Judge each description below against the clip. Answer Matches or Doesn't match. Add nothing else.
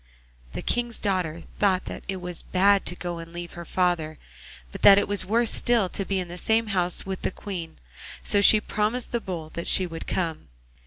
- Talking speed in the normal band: Doesn't match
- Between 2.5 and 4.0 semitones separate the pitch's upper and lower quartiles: Matches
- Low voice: Doesn't match